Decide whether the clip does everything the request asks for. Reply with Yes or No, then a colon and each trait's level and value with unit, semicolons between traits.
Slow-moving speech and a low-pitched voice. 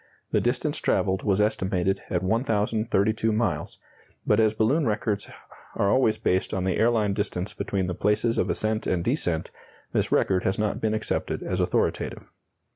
No: average, 160 wpm; low, 105 Hz